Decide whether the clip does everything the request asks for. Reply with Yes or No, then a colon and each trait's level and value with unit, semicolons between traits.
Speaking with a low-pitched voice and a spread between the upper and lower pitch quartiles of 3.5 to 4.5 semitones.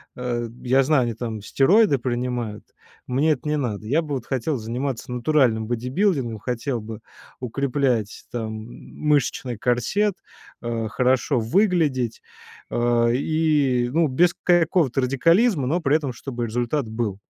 Yes: low, 125 Hz; average, 4.1 semitones